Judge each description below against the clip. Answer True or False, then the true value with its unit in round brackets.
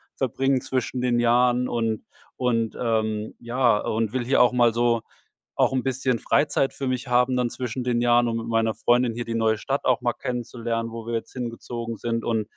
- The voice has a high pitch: False (120 Hz)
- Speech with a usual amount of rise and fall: False (1.6 semitones)